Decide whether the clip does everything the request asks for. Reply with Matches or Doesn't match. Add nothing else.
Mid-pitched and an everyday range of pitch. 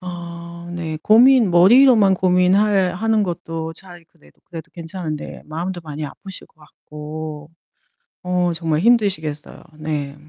Matches